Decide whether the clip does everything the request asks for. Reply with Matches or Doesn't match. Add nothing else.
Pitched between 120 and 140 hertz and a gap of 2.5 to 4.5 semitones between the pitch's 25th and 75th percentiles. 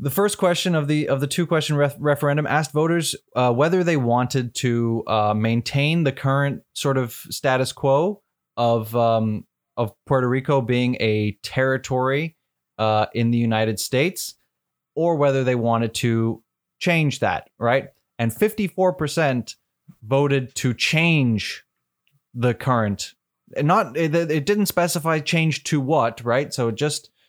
Doesn't match